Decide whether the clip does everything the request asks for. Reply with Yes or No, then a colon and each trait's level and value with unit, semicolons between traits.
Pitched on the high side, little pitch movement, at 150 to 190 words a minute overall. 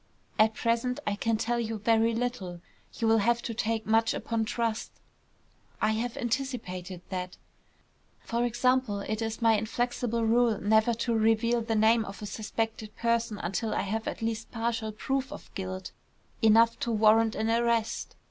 Yes: high, 225 Hz; narrow, 1.4 semitones; average, 165 wpm